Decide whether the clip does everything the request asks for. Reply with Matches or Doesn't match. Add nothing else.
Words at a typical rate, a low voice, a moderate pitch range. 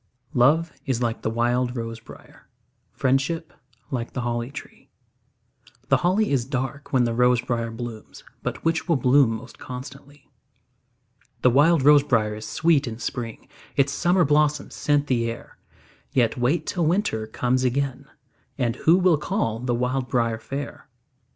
Matches